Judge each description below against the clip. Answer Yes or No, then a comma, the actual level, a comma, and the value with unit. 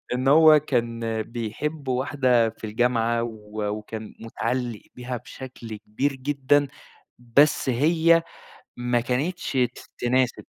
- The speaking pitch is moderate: No, low, 125 Hz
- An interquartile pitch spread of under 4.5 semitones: Yes, average, 3.4 semitones